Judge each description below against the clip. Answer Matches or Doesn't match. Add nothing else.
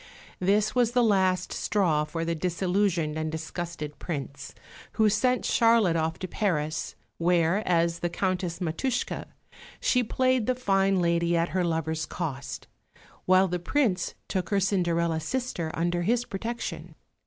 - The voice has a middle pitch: Matches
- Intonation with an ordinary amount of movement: Matches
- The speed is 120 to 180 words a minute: Matches